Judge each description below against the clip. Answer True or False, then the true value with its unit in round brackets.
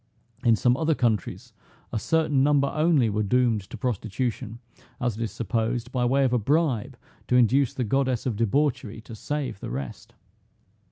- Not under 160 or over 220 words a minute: True (170 wpm)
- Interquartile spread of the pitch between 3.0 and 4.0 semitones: True (3.6 semitones)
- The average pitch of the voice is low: True (125 Hz)